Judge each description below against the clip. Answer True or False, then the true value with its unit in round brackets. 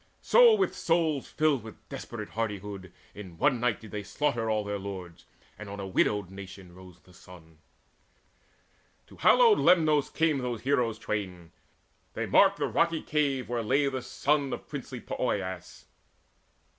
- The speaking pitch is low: True (115 Hz)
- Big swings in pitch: True (6.8 semitones)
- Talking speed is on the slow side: False (155 wpm)